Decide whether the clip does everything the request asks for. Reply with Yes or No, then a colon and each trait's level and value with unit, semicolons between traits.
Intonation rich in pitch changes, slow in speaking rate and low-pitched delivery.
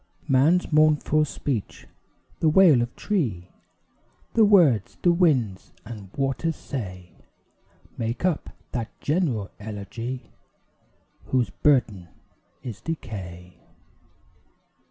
Yes: wide, 6.9 semitones; slow, 95 wpm; low, 130 Hz